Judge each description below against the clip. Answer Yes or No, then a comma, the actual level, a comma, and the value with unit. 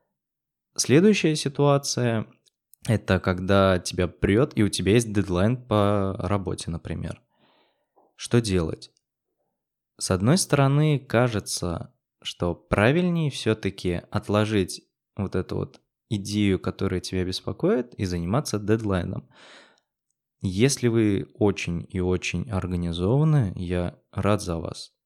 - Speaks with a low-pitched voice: Yes, low, 100 Hz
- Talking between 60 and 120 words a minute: Yes, slow, 110 wpm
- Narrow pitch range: No, average, 4.7 semitones